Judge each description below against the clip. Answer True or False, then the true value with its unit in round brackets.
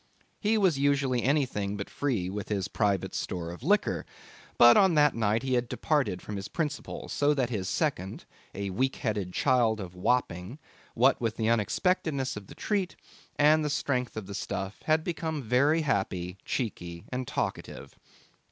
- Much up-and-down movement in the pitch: True (6.4 semitones)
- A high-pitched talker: False (120 Hz)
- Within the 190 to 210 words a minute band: False (170 wpm)